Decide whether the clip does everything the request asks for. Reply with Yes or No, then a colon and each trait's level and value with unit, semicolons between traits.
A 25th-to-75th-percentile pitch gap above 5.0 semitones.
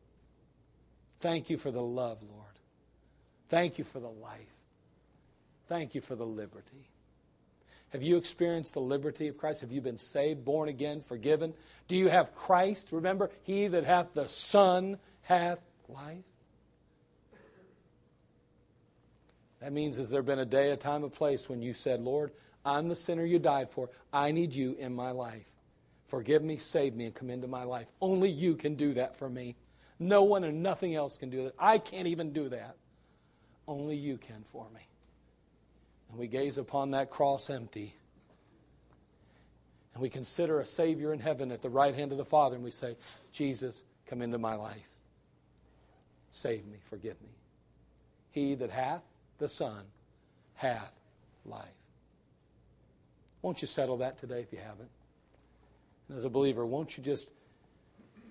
Yes: wide, 5.5 semitones